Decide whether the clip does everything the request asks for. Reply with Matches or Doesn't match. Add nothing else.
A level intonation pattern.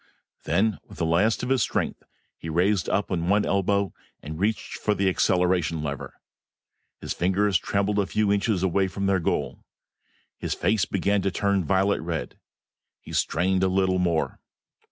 Matches